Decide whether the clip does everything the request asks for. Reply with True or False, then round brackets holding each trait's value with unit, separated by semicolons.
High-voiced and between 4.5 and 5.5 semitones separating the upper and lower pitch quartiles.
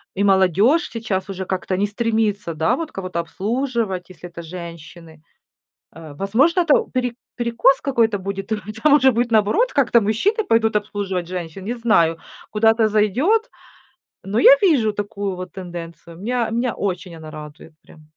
True (205 Hz; 4.8 semitones)